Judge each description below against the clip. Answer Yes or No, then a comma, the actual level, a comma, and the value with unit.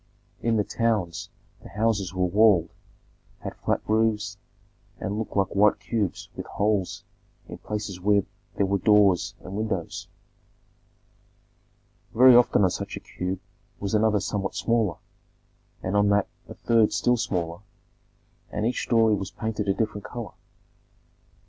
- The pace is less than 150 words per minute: Yes, average, 140 wpm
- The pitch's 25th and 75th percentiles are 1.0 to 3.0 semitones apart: Yes, narrow, 2.4 semitones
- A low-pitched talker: Yes, low, 105 Hz